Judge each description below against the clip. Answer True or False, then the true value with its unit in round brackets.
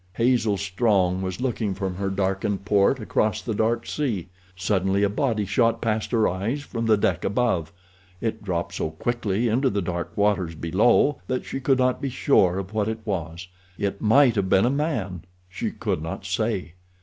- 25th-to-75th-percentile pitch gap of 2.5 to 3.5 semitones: False (3.9 semitones)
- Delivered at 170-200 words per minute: True (180 wpm)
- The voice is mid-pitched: False (100 Hz)